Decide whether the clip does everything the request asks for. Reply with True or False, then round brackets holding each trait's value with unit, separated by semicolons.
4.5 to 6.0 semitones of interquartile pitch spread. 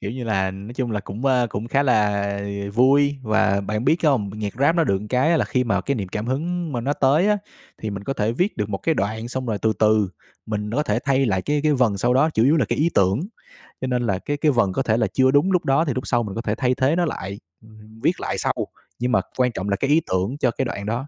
True (4.9 semitones)